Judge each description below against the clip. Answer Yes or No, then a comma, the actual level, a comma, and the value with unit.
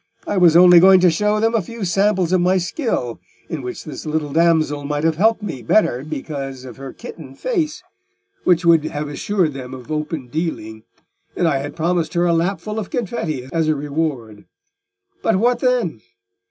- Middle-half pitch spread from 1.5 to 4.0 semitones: No, average, 4.7 semitones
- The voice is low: No, medium, 165 Hz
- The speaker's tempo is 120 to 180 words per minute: No, average, 190 wpm